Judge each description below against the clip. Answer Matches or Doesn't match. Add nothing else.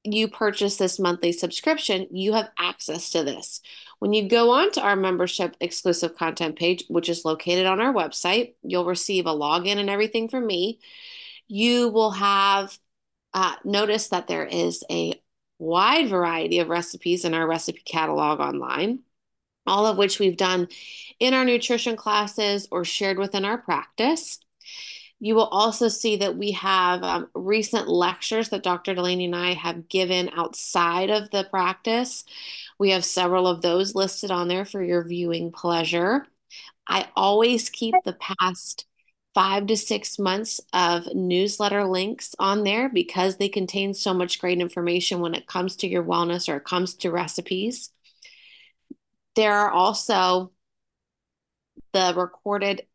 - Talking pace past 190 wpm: Doesn't match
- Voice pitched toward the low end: Doesn't match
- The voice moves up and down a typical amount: Matches